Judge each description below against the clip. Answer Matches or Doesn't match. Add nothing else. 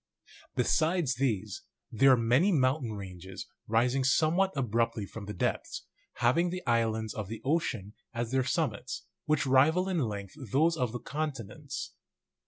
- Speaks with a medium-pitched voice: Doesn't match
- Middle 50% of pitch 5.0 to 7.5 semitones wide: Matches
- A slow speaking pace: Doesn't match